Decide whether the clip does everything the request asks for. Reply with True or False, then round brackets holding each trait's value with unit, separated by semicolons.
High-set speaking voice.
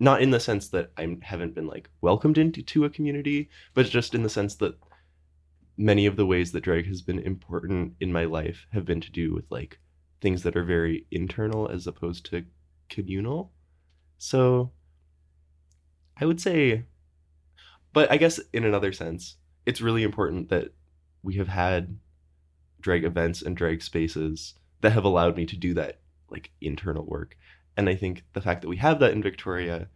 False (85 Hz)